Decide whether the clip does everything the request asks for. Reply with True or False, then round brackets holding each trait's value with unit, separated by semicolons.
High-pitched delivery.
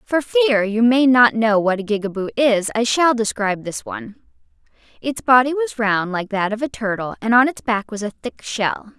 True (230 Hz)